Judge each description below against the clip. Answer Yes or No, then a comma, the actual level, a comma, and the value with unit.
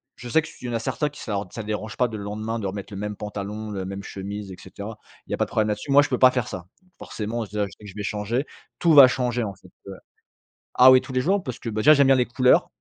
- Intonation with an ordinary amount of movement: Yes, average, 3.7 semitones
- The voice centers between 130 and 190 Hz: No, low, 110 Hz